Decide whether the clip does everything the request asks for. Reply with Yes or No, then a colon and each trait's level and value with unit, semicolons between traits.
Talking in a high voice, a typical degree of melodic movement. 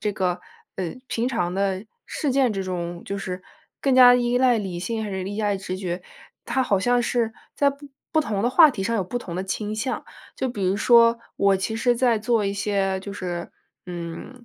Yes: high, 205 Hz; average, 4.3 semitones